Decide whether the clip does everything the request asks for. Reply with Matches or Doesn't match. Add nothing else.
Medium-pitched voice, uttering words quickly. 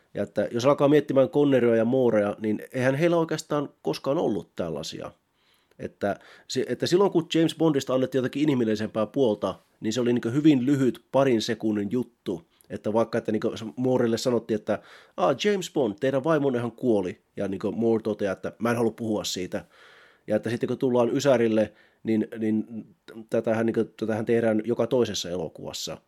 Doesn't match